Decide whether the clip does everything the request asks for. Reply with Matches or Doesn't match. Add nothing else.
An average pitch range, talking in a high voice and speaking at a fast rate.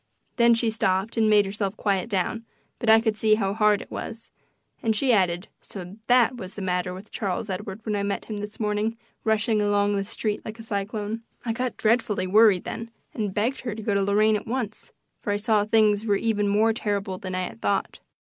Doesn't match